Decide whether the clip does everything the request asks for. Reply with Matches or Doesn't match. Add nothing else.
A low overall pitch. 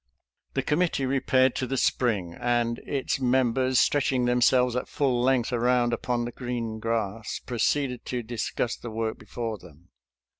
Matches